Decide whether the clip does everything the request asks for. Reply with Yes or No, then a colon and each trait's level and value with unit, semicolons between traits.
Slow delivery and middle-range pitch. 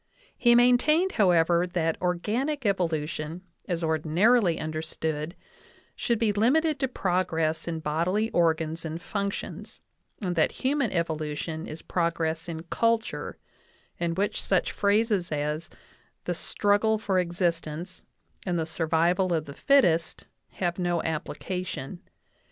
Yes: slow, 125 wpm; medium, 175 Hz